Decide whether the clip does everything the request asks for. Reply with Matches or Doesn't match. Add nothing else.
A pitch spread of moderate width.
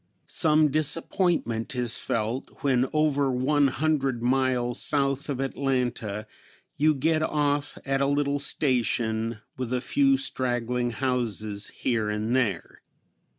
Matches